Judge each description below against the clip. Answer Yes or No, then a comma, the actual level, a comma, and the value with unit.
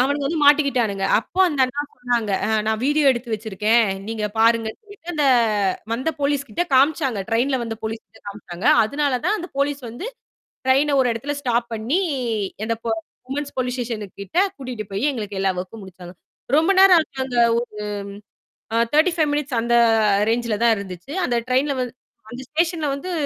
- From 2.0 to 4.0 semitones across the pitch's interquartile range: No, average, 4.5 semitones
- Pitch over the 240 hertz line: Yes, very high, 250 Hz